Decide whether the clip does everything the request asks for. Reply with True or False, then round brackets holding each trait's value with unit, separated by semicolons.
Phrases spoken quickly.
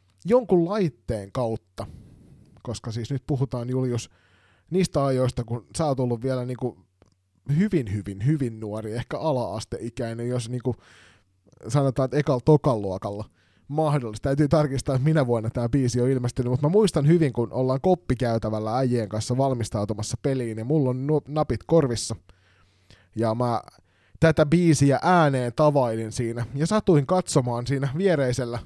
False (140 wpm)